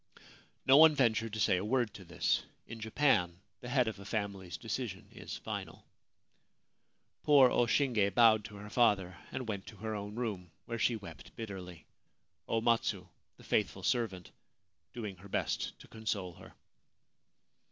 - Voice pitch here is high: No, low, 110 Hz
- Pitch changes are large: No, average, 3.5 semitones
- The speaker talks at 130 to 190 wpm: Yes, average, 160 wpm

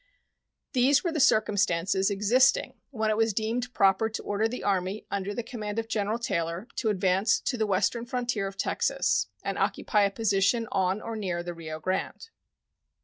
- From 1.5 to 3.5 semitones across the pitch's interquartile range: Yes, average, 3.1 semitones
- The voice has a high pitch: Yes, high, 210 Hz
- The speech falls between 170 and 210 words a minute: Yes, average, 175 wpm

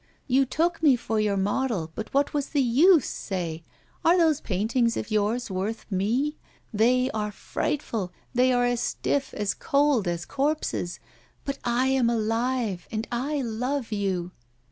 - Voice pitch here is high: Yes, high, 240 Hz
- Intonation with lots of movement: No, average, 4.7 semitones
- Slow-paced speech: No, average, 155 wpm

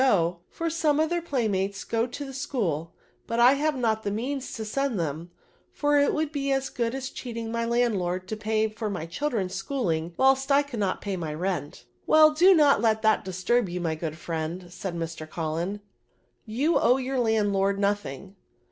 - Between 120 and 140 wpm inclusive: No, average, 200 wpm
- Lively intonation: Yes, wide, 6.7 semitones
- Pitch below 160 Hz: No, high, 220 Hz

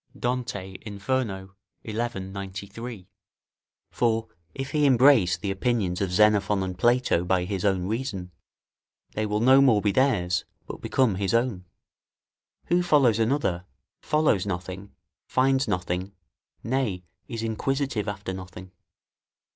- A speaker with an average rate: No, slow, 125 wpm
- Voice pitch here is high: No, low, 105 Hz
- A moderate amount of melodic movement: Yes, average, 4.9 semitones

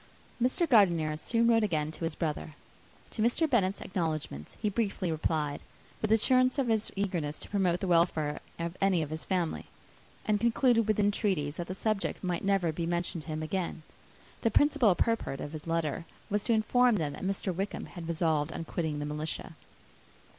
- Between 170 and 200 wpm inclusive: Yes, average, 185 wpm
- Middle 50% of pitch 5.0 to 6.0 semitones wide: Yes, average, 5.3 semitones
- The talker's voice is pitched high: No, medium, 180 Hz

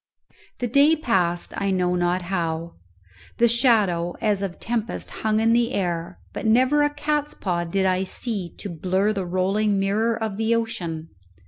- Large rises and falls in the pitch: No, average, 4.6 semitones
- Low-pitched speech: No, high, 200 Hz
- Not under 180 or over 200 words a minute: No, average, 165 wpm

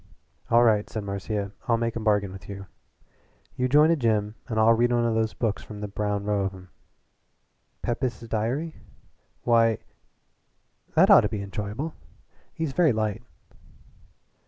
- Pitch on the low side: Yes, low, 110 Hz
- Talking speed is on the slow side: No, average, 160 wpm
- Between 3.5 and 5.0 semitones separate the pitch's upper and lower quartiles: No, narrow, 2.5 semitones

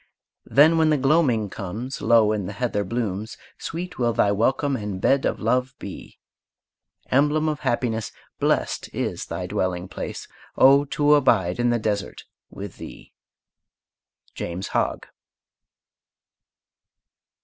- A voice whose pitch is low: Yes, low, 120 Hz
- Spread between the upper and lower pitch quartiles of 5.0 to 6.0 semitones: Yes, wide, 5.4 semitones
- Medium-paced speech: No, slow, 125 wpm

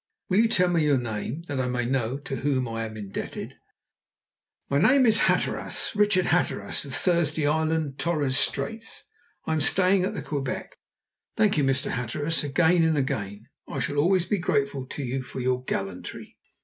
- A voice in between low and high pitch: Yes, medium, 145 Hz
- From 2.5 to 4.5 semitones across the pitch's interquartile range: No, average, 5.2 semitones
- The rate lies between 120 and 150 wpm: No, average, 175 wpm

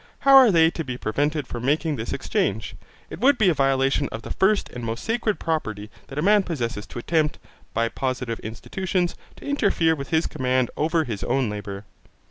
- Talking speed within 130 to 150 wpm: No, average, 195 wpm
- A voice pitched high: No, medium, 145 Hz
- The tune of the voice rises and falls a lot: Yes, wide, 6.5 semitones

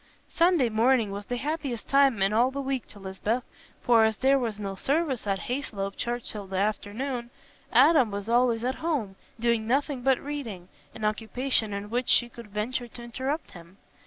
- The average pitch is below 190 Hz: No, high, 235 Hz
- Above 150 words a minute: Yes, average, 185 wpm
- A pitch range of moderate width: Yes, average, 4.0 semitones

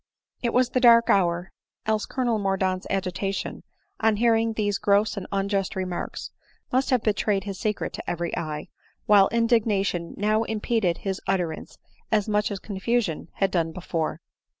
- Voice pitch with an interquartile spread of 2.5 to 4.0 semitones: Yes, average, 3.1 semitones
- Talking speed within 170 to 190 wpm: No, average, 155 wpm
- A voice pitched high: Yes, high, 200 Hz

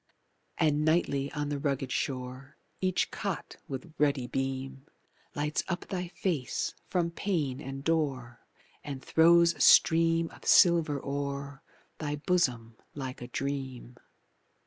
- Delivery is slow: Yes, slow, 125 wpm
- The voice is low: No, medium, 145 Hz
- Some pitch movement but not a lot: Yes, average, 3.6 semitones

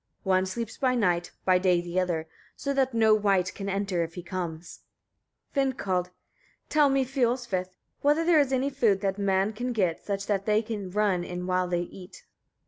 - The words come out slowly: No, average, 195 wpm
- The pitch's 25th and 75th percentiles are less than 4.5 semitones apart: No, average, 4.9 semitones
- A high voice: Yes, high, 195 Hz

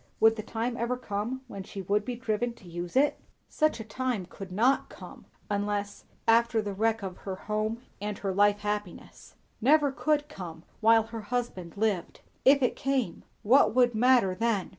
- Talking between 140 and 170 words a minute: No, average, 180 wpm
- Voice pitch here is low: No, high, 220 Hz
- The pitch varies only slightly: No, average, 3.4 semitones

